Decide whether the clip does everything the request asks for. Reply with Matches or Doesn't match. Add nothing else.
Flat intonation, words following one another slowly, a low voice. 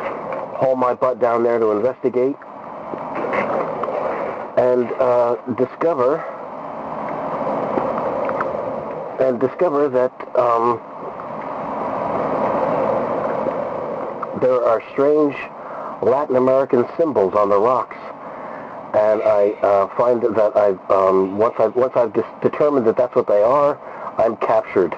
Matches